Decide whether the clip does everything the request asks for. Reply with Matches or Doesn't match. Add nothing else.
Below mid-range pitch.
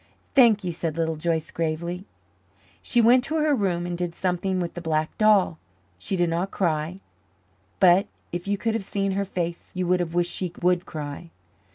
Doesn't match